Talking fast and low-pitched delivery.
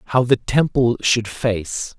No: average, 150 wpm; low, 120 Hz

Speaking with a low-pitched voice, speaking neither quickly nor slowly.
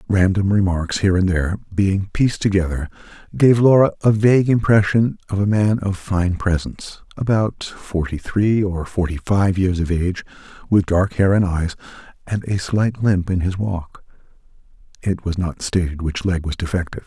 Yes: very low, 95 Hz; average, 165 wpm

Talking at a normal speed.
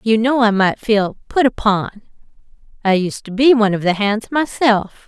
Yes: average, 190 wpm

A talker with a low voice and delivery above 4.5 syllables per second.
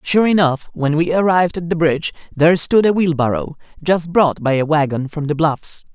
No: medium, 160 Hz; 5.3 syllables/s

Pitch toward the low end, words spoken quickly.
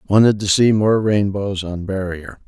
No: low, 100 Hz; average, 170 wpm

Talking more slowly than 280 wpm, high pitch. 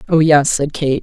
No: fast, 235 wpm; medium, 150 Hz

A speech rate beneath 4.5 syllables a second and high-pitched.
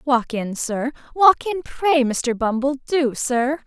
Yes: 3.7 syllables/s; very high, 270 Hz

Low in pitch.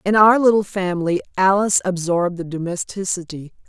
No: medium, 185 Hz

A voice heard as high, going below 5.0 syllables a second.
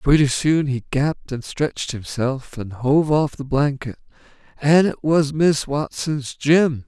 No: medium, 140 Hz; 4.0 syllables/s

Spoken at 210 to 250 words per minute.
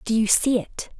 Yes: fast, 240 wpm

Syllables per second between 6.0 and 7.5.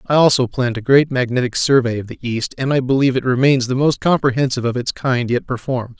Yes: 6.4 syllables/s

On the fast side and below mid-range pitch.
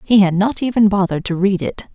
No: fast, 245 wpm; high, 200 Hz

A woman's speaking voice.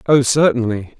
No: male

